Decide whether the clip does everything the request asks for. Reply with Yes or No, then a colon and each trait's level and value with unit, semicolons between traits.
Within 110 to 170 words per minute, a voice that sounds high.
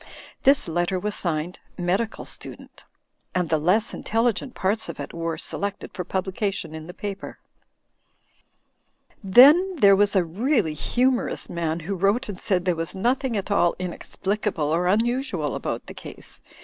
Yes: average, 160 wpm; high, 195 Hz